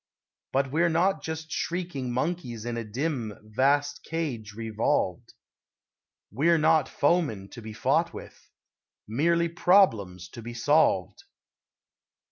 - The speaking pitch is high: No, low, 135 Hz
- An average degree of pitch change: No, wide, 6.7 semitones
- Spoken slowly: Yes, slow, 115 wpm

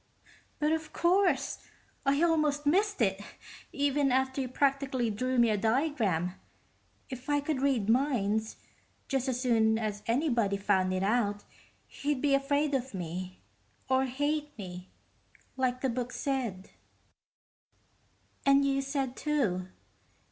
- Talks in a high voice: Yes, very high, 260 Hz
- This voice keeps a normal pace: No, slow, 130 wpm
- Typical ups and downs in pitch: Yes, average, 4.7 semitones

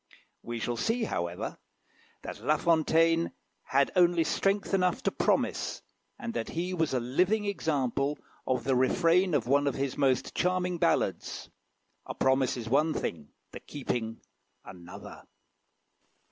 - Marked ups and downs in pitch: Yes, wide, 5.9 semitones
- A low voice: No, medium, 150 Hz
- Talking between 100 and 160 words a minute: Yes, average, 140 wpm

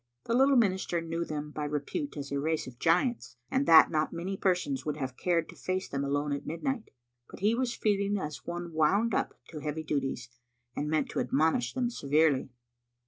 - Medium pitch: Yes, medium, 160 Hz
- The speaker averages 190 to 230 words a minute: Yes, average, 195 wpm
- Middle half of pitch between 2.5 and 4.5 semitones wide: No, average, 5.2 semitones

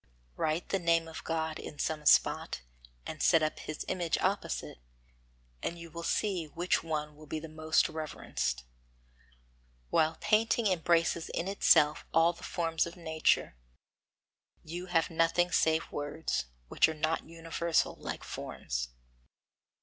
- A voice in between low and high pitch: Yes, medium, 165 Hz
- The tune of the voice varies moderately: No, narrow, 1.5 semitones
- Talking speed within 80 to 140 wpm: Yes, slow, 135 wpm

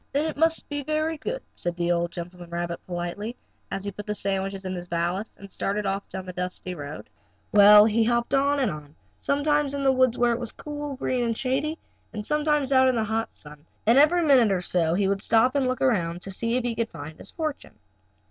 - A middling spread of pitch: No, wide, 7.0 semitones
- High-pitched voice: Yes, high, 220 Hz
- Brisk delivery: Yes, fast, 235 wpm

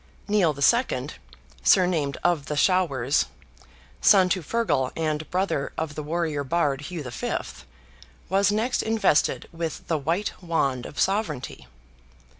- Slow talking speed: Yes, slow, 125 wpm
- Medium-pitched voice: Yes, medium, 165 Hz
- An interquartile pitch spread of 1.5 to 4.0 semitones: No, average, 4.6 semitones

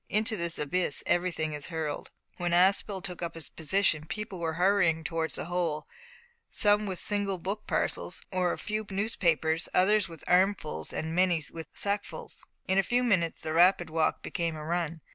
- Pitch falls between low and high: Yes, medium, 175 Hz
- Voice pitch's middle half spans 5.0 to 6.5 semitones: No, average, 3.3 semitones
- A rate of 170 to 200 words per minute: Yes, average, 175 wpm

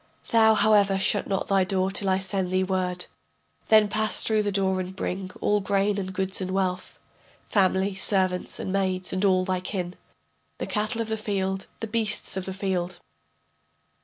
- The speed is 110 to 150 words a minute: No, average, 190 wpm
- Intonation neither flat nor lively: No, narrow, 1.7 semitones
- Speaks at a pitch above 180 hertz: Yes, high, 190 Hz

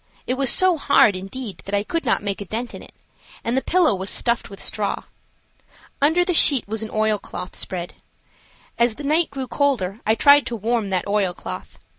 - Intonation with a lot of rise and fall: Yes, wide, 5.8 semitones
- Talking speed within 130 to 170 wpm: No, average, 195 wpm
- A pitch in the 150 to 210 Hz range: No, high, 225 Hz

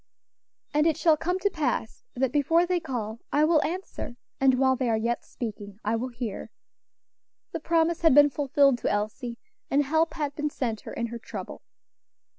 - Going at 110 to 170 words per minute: No, average, 185 wpm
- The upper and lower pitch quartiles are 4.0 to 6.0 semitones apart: Yes, average, 5.2 semitones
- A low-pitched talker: No, very high, 270 Hz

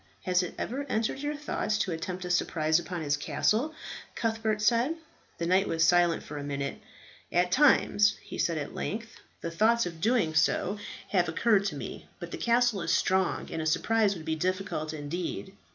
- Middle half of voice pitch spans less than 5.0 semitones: No, wide, 5.4 semitones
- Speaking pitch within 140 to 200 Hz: Yes, medium, 185 Hz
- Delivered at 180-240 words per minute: Yes, average, 185 wpm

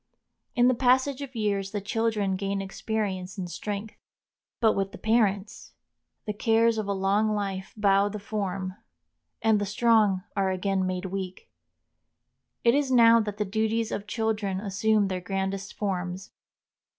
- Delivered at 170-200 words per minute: No, average, 150 wpm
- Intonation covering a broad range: No, narrow, 2.4 semitones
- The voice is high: Yes, high, 205 Hz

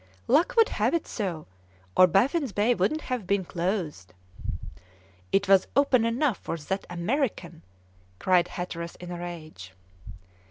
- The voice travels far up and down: Yes, wide, 6.1 semitones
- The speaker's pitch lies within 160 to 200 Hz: Yes, high, 190 Hz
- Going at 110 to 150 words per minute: Yes, slow, 135 wpm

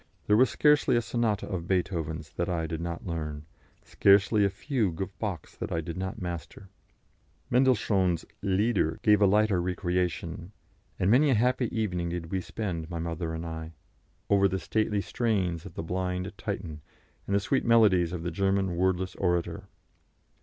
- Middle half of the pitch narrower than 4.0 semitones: Yes, average, 3.5 semitones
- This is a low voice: Yes, very low, 95 Hz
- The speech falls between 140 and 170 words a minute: Yes, average, 165 wpm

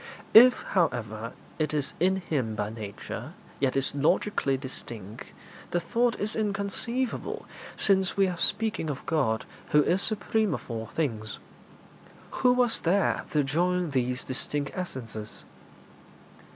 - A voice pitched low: No, medium, 155 Hz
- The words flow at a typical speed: No, slow, 130 wpm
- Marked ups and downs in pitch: Yes, wide, 7.9 semitones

